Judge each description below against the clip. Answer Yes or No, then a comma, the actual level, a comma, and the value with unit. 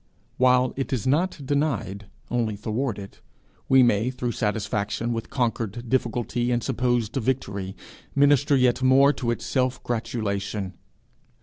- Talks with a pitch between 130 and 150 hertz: No, low, 120 Hz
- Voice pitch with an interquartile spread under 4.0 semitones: Yes, average, 3.3 semitones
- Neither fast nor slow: No, slow, 125 wpm